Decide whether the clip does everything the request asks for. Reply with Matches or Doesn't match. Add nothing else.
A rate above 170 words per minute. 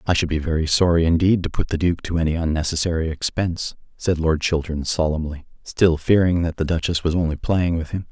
Matches